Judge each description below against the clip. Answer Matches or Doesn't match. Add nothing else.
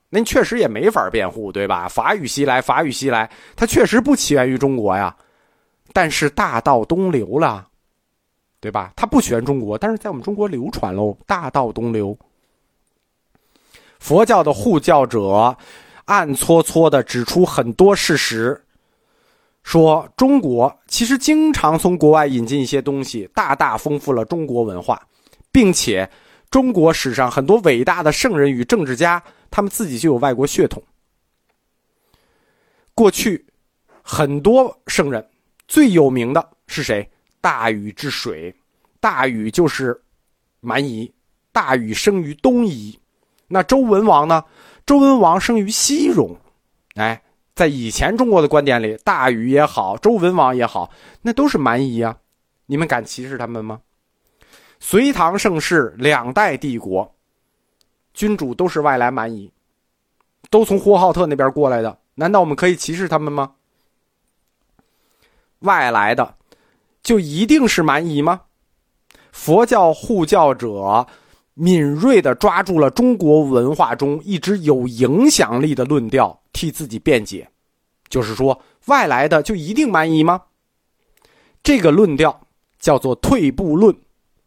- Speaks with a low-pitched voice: Doesn't match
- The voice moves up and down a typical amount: Doesn't match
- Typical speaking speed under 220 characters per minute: Matches